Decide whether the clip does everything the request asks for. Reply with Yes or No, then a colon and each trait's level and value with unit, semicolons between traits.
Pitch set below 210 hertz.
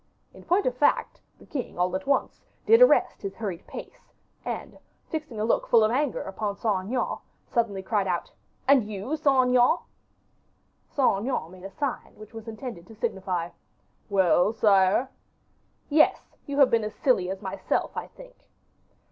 No: high, 220 Hz